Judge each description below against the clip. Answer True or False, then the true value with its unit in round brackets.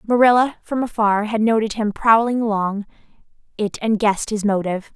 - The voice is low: False (215 Hz)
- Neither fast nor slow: True (155 wpm)